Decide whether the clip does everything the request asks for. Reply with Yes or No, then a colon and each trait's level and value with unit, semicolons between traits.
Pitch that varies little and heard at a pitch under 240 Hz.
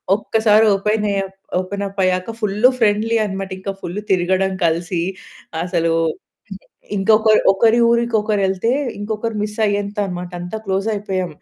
Yes: narrow, 2.3 semitones; high, 200 Hz